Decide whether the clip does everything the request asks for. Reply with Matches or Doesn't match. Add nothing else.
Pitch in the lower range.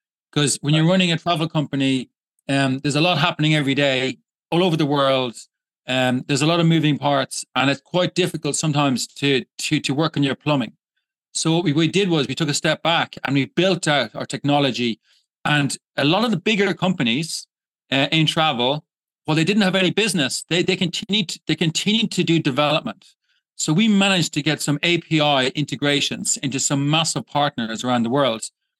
Doesn't match